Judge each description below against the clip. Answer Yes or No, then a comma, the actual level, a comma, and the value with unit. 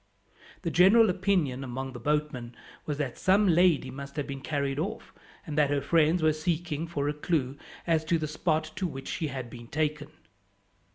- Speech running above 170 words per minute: Yes, average, 185 wpm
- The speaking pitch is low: No, medium, 150 Hz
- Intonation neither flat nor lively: Yes, average, 3.4 semitones